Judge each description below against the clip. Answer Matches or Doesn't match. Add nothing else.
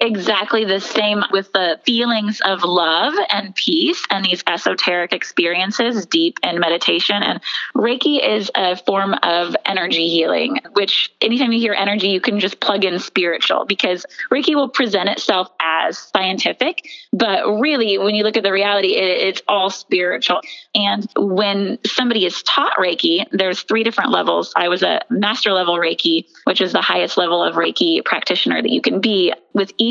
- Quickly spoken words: Doesn't match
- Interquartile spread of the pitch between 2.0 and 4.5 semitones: Matches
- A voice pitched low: Doesn't match